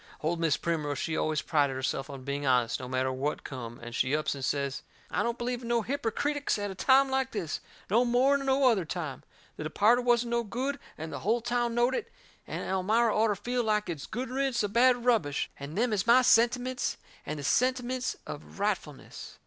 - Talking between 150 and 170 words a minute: No, fast, 205 wpm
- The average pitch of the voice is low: No, high, 215 Hz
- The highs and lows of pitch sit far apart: Yes, wide, 8.5 semitones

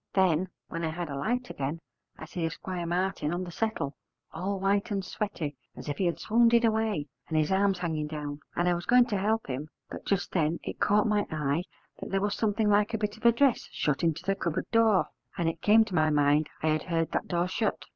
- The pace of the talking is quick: Yes, fast, 235 wpm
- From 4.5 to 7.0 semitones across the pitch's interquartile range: Yes, average, 4.8 semitones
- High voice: No, medium, 180 Hz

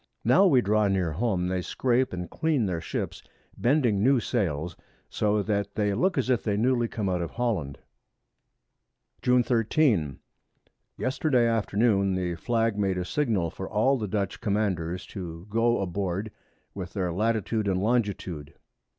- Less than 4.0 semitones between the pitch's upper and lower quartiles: No, average, 4.4 semitones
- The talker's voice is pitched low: Yes, low, 105 Hz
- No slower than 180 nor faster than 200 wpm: No, average, 150 wpm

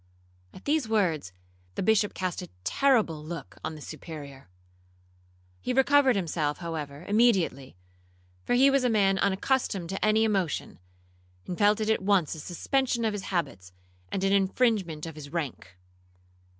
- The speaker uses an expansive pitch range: Yes, wide, 5.8 semitones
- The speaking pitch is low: No, high, 190 Hz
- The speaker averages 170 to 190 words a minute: No, average, 150 wpm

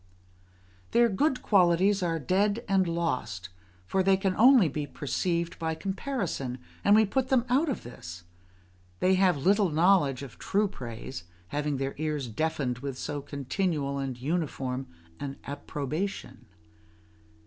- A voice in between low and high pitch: Yes, medium, 165 Hz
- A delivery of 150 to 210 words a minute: No, slow, 135 wpm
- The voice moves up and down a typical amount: No, wide, 6.1 semitones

